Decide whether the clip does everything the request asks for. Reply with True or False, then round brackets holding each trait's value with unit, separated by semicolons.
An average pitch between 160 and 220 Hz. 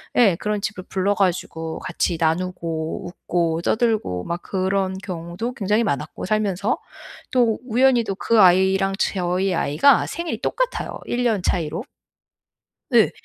True (190 Hz)